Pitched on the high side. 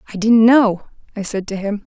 Yes: high, 210 Hz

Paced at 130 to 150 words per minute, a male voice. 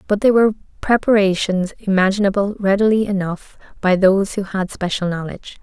No: average, 140 wpm; female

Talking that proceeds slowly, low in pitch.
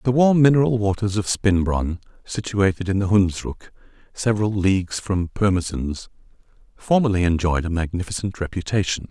Yes: slow, 125 wpm; low, 100 Hz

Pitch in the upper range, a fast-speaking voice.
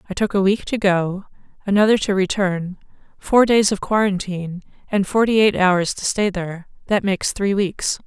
No: high, 195 Hz; average, 180 wpm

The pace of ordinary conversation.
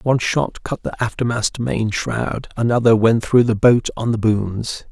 Yes: average, 185 wpm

